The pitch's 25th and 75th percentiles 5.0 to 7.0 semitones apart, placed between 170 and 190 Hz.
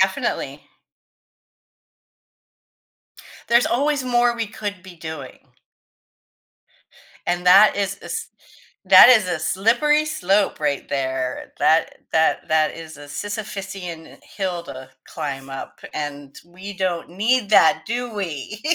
Yes: wide, 5.4 semitones; medium, 185 Hz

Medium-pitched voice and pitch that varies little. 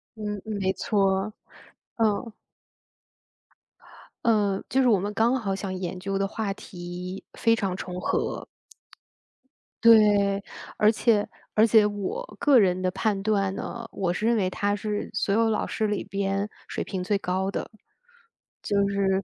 No: high, 200 Hz; narrow, 2.0 semitones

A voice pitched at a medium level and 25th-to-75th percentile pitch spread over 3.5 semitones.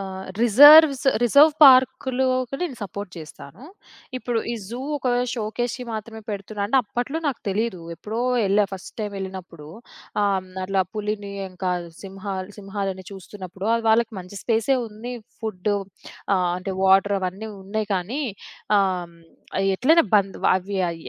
No: high, 205 Hz; average, 4.1 semitones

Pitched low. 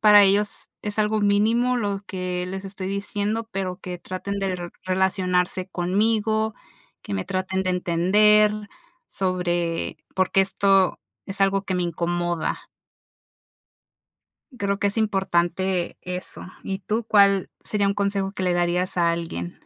No: high, 190 Hz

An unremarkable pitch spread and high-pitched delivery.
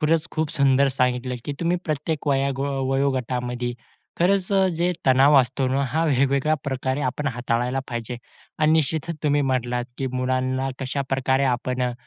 No: average, 3.0 semitones; low, 135 Hz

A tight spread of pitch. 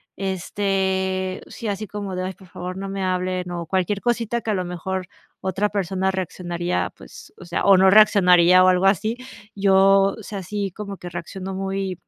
Yes: narrow, 1.3 semitones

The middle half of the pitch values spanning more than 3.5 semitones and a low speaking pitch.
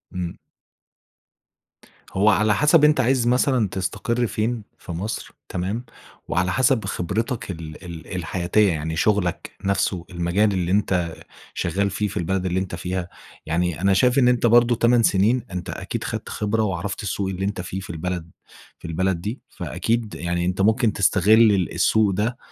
Yes: average, 4.0 semitones; low, 100 Hz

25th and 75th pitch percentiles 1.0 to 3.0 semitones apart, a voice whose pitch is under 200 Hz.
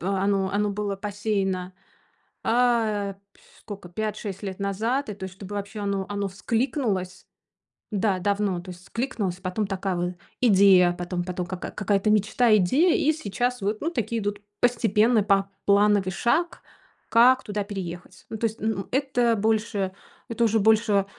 No: average, 2.7 semitones; high, 205 Hz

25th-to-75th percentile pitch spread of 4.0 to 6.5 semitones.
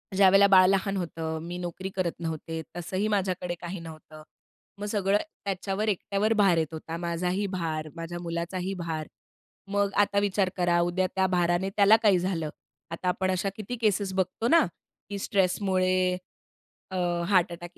No: narrow, 2.4 semitones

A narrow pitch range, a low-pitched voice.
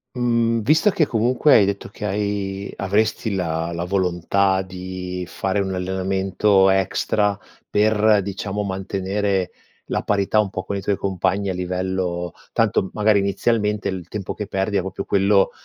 Yes: narrow, 1.9 semitones; low, 100 Hz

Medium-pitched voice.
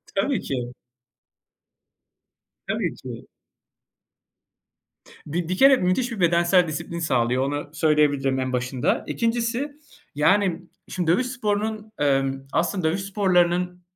Yes: medium, 175 Hz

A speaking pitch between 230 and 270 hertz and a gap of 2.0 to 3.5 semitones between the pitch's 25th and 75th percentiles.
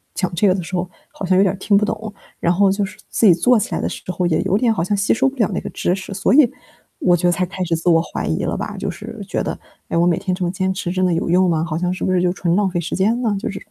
No: medium, 185 Hz; narrow, 2.4 semitones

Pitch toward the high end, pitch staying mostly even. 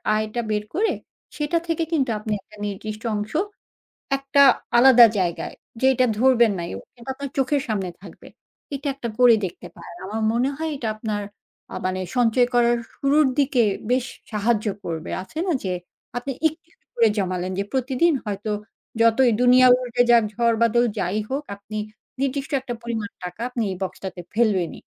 No: high, 235 Hz; average, 4.1 semitones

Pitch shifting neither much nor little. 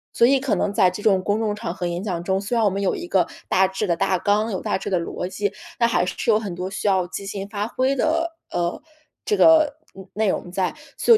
Yes: average, 3.2 semitones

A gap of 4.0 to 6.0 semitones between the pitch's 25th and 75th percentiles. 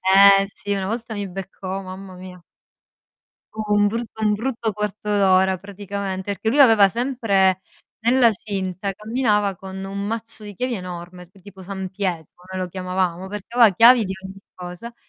No: narrow, 2.5 semitones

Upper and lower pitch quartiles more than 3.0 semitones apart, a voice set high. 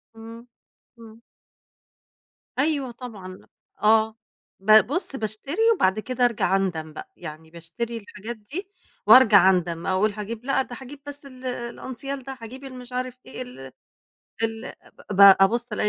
Yes: average, 4.3 semitones; high, 230 Hz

